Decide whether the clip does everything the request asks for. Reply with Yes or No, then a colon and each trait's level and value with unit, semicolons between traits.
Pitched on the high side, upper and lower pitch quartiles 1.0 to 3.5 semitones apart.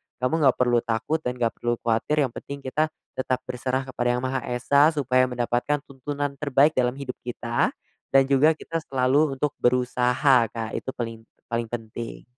No: low, 130 Hz; narrow, 2.5 semitones